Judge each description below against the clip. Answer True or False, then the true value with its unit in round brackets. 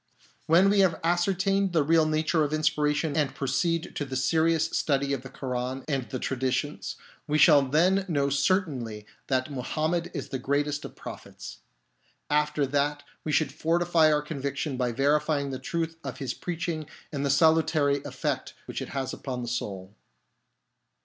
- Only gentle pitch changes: False (3.2 semitones)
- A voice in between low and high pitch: True (150 Hz)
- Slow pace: False (165 wpm)